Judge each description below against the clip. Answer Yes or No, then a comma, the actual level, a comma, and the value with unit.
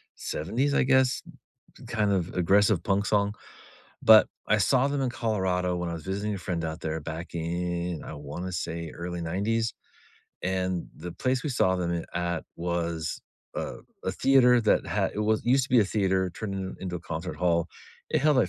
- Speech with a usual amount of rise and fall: Yes, average, 4.1 semitones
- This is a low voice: Yes, very low, 95 Hz